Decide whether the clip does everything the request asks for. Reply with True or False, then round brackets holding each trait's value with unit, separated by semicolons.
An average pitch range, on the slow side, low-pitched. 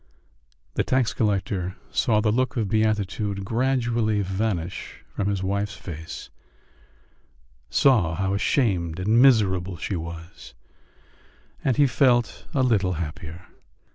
True (4.0 semitones; 115 wpm; 100 Hz)